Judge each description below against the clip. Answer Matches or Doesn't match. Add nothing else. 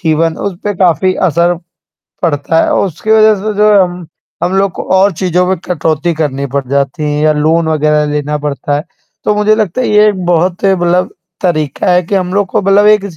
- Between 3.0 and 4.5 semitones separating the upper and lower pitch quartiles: Matches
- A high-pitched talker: Doesn't match